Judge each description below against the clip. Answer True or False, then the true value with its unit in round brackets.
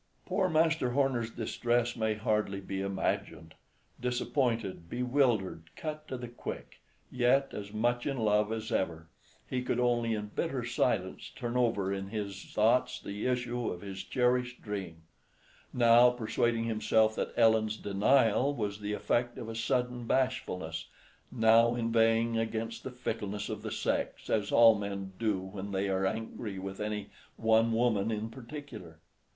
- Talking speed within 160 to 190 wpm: False (150 wpm)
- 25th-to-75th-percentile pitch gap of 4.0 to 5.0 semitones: False (3.2 semitones)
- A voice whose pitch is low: True (115 Hz)